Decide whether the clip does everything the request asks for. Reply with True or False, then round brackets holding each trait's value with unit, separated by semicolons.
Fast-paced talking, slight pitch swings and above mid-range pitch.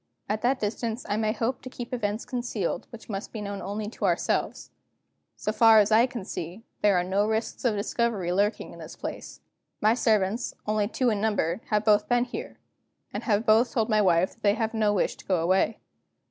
True (215 wpm; 2.1 semitones; 215 Hz)